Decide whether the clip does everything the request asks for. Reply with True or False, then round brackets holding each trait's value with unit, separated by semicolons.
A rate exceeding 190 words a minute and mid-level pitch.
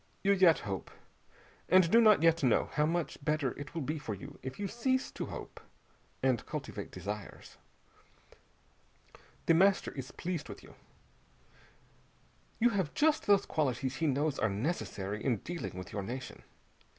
False (155 wpm; 150 Hz)